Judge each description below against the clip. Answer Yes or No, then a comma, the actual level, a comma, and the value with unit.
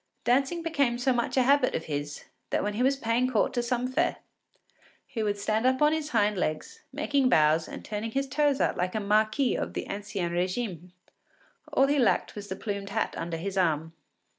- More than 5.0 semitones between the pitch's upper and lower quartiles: Yes, wide, 5.4 semitones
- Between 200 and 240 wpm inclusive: Yes, fast, 205 wpm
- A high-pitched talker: Yes, high, 225 Hz